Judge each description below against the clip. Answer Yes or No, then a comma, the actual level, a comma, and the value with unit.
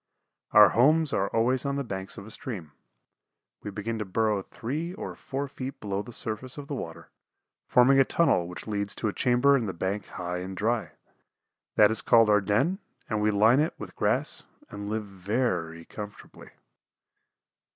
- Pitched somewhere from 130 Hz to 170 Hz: No, low, 110 Hz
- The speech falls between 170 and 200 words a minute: Yes, average, 180 wpm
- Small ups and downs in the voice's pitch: No, average, 4.4 semitones